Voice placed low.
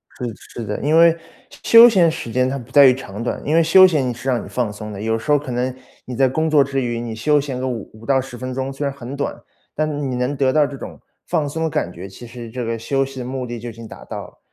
Yes: low, 130 Hz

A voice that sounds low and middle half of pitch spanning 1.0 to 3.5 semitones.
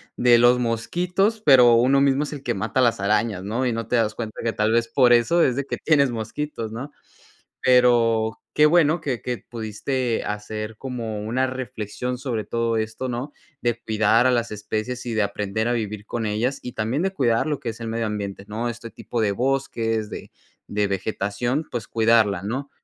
Yes: low, 115 Hz; average, 2.9 semitones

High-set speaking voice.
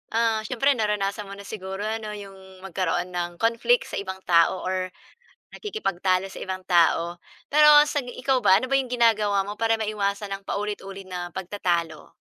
Yes: high, 200 Hz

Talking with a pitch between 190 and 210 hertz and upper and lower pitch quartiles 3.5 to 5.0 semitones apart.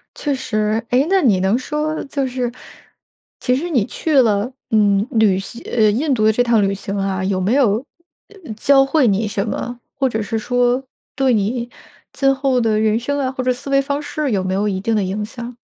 No: high, 235 Hz; average, 4.3 semitones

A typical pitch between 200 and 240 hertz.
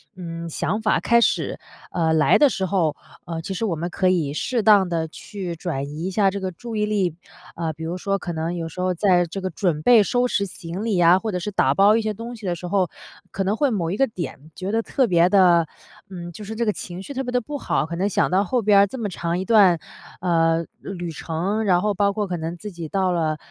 No: medium, 185 Hz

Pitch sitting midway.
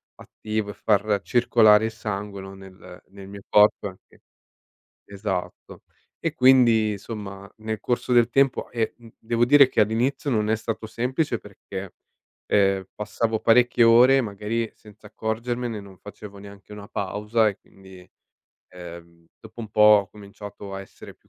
No: low, 105 Hz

